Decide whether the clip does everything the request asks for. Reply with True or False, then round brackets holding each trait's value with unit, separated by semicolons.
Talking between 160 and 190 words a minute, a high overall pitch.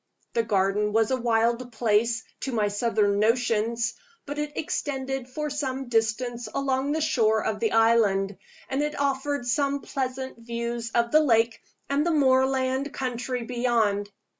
False (150 wpm; 240 Hz)